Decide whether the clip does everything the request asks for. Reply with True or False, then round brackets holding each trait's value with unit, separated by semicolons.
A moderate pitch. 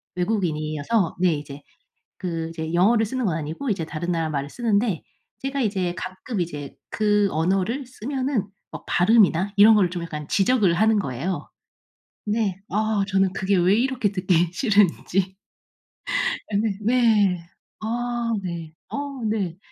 False (195 Hz)